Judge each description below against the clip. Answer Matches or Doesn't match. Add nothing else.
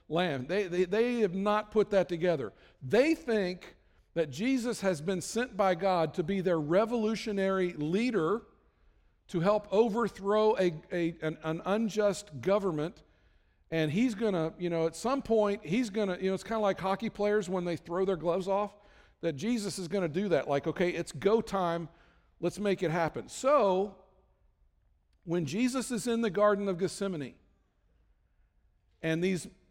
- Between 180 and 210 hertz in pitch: Matches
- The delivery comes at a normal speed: Matches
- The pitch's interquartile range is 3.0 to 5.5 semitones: Matches